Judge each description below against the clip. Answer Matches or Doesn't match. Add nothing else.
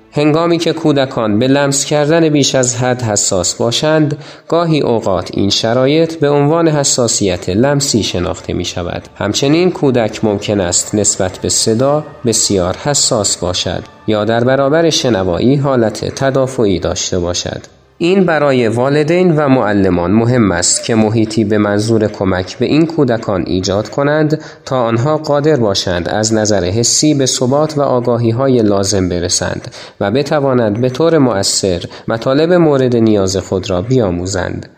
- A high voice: Doesn't match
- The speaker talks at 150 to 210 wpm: Doesn't match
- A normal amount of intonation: Doesn't match